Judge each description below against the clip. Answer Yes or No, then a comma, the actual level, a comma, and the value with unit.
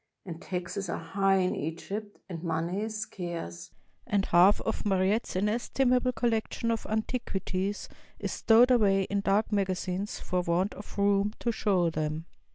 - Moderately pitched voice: No, high, 195 Hz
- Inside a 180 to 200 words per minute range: No, average, 150 wpm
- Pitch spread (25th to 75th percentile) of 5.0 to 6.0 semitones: No, average, 3.2 semitones